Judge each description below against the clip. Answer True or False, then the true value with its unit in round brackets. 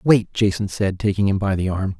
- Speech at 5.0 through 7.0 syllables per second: True (5.2 syllables/s)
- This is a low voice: True (100 Hz)